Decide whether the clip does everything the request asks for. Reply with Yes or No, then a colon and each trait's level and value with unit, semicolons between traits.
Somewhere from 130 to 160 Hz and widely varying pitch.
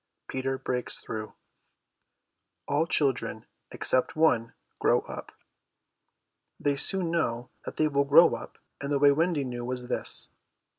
No: medium, 140 Hz; average, 3.8 semitones